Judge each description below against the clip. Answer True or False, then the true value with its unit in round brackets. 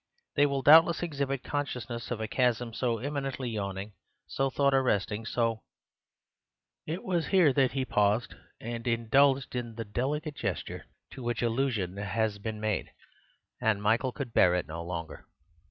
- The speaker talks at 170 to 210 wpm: False (155 wpm)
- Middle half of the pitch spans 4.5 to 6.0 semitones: False (4.1 semitones)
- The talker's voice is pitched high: False (120 Hz)